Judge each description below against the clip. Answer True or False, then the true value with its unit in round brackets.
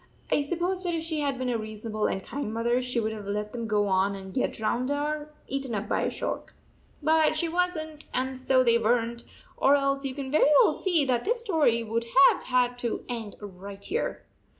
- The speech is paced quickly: True (235 wpm)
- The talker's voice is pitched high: True (250 Hz)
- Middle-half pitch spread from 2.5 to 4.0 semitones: False (5.2 semitones)